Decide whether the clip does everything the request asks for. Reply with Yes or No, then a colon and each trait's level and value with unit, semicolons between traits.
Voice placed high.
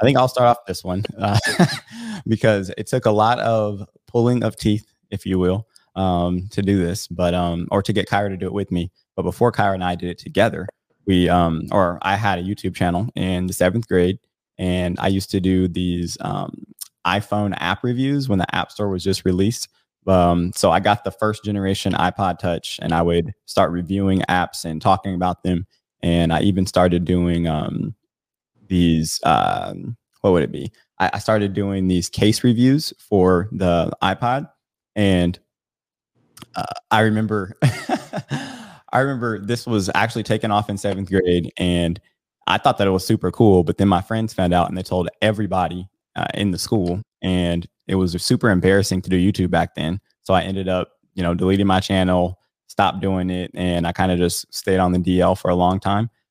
No: very low, 95 Hz